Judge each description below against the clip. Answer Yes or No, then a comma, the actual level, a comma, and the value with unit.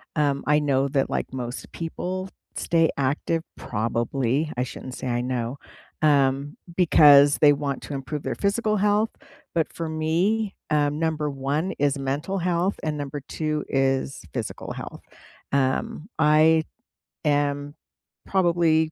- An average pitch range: Yes, average, 3.0 semitones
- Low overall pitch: No, medium, 150 Hz